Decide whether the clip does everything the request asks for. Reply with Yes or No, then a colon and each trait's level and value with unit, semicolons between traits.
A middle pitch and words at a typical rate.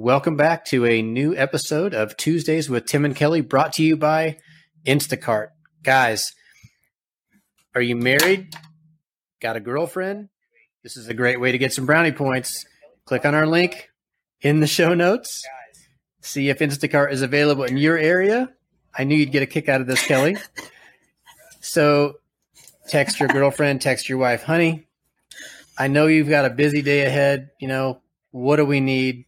Yes: medium, 145 Hz; average, 170 wpm